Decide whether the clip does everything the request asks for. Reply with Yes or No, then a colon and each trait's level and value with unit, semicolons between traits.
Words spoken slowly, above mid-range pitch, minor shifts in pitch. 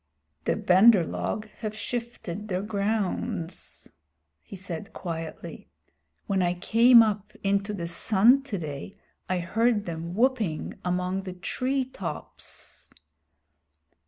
No: slow, 110 wpm; high, 200 Hz; average, 3.8 semitones